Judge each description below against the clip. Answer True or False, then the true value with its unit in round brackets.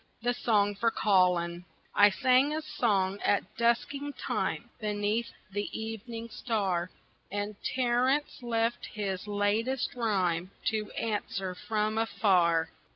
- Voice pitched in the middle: False (210 Hz)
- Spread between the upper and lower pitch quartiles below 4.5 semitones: True (3.2 semitones)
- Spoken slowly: True (115 wpm)